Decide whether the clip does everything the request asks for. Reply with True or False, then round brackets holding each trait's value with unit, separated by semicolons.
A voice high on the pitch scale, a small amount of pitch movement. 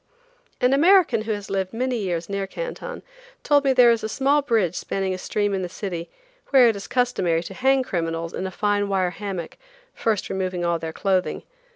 False (200 Hz; 5.3 semitones)